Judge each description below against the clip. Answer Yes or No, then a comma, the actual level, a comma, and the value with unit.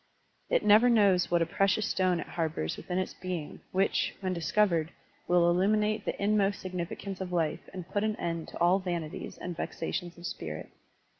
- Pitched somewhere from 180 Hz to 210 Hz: Yes, medium, 185 Hz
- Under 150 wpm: No, average, 180 wpm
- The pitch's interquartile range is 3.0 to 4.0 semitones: No, narrow, 2.6 semitones